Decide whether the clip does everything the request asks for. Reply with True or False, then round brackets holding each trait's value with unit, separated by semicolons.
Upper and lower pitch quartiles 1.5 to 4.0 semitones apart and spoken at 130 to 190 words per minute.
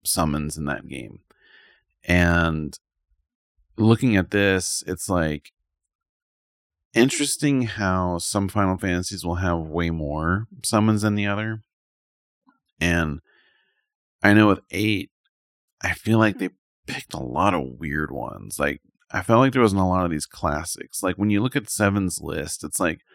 False (4.5 semitones; 150 wpm)